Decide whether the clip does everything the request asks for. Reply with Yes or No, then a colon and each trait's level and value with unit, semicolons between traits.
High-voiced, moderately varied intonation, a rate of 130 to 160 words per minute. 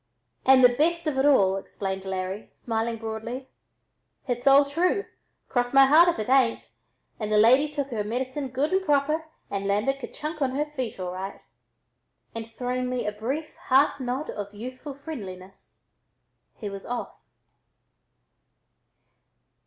Yes: very high, 255 Hz; average, 4.9 semitones; average, 150 wpm